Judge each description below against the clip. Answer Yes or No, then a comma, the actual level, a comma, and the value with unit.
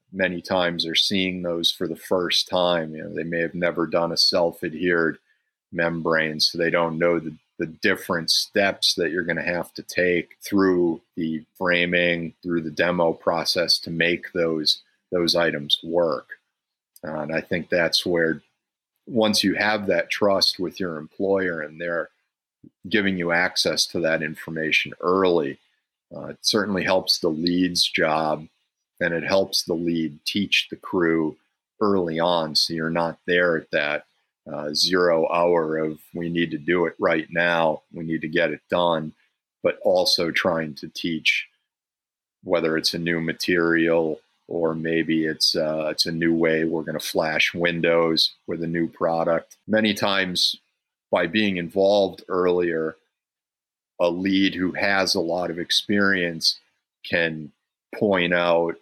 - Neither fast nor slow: Yes, average, 160 wpm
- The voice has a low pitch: Yes, very low, 85 Hz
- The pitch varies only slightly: Yes, narrow, 1.6 semitones